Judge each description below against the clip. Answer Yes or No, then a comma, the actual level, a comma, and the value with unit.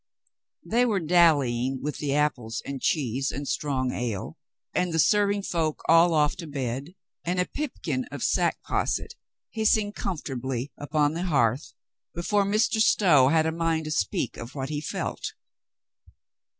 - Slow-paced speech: No, average, 155 wpm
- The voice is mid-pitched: Yes, medium, 155 Hz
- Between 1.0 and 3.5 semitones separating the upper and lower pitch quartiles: No, average, 5.0 semitones